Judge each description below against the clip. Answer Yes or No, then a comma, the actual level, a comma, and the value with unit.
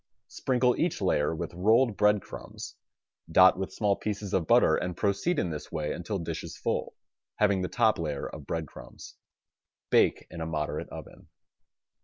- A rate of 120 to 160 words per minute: No, average, 170 wpm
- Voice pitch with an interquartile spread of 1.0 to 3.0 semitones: No, average, 4.5 semitones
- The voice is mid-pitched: No, very low, 95 Hz